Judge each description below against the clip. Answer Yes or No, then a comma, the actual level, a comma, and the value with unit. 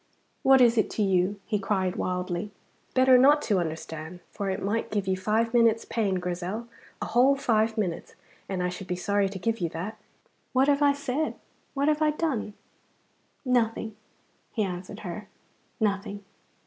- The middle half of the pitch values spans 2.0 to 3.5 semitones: No, average, 4.5 semitones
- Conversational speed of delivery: Yes, average, 170 wpm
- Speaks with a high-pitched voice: Yes, high, 210 Hz